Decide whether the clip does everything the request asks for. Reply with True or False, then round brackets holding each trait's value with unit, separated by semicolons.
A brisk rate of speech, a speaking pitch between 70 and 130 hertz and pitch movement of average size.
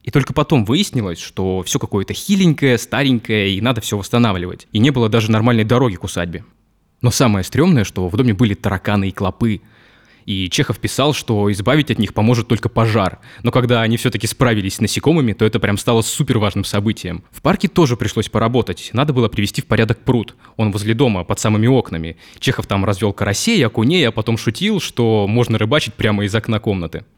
True (190 wpm; 115 Hz; 3.2 semitones)